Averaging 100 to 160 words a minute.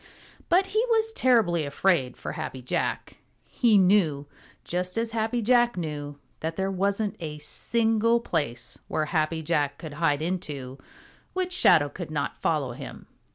Yes: average, 150 wpm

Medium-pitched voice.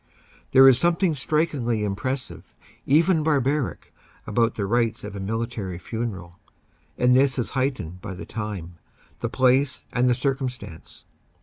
No: low, 125 Hz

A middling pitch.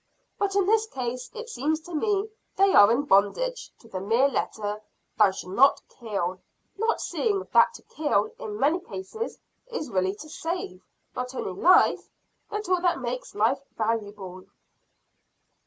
No: very high, 275 Hz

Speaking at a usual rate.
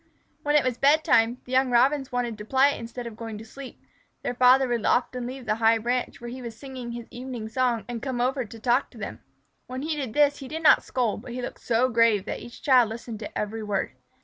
No: fast, 245 wpm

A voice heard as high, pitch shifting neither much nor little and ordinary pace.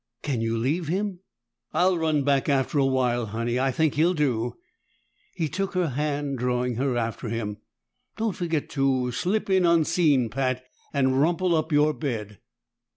No: medium, 140 Hz; average, 4.8 semitones; average, 160 wpm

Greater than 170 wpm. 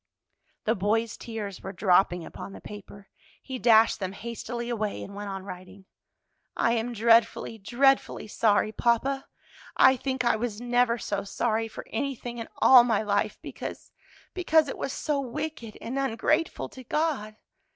No: average, 155 wpm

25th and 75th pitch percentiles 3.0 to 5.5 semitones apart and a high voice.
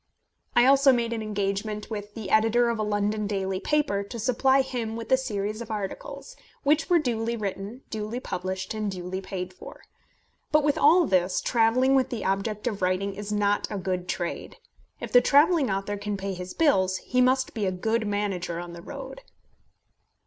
Yes: average, 4.1 semitones; high, 210 Hz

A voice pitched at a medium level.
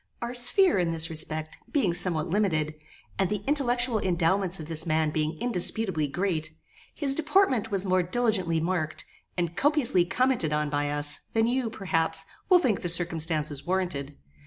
Yes: medium, 180 Hz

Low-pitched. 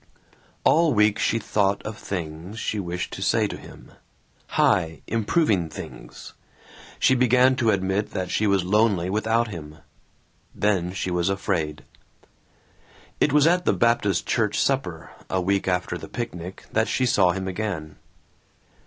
Yes: low, 100 Hz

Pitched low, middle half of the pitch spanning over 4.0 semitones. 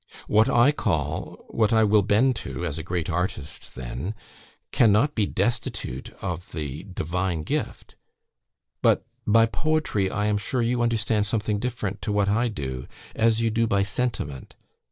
Yes: low, 105 Hz; average, 4.5 semitones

